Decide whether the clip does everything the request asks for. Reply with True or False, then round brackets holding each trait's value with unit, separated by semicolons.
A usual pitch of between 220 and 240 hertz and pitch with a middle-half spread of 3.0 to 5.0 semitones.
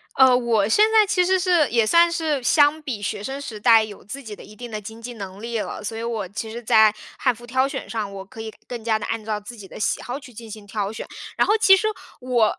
True (230 Hz; 4.2 semitones)